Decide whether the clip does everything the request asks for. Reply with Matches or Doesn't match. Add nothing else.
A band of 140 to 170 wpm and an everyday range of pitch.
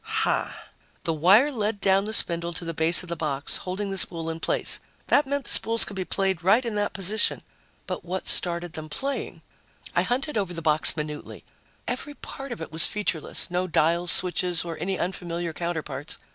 Doesn't match